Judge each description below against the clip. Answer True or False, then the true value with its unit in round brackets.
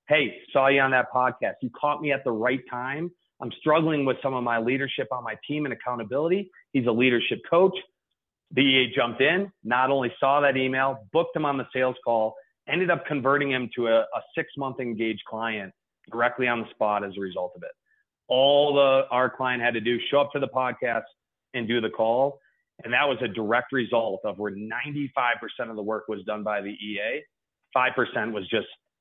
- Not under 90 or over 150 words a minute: False (205 wpm)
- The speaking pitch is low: True (130 Hz)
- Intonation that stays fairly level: False (3.4 semitones)